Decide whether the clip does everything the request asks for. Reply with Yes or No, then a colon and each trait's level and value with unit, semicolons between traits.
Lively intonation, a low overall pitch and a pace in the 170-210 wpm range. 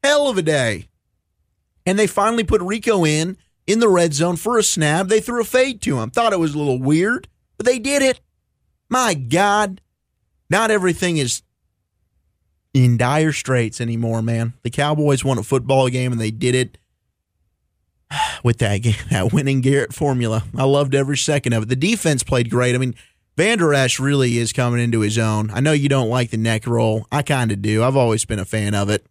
Yes: wide, 6.8 semitones; low, 130 Hz; average, 200 wpm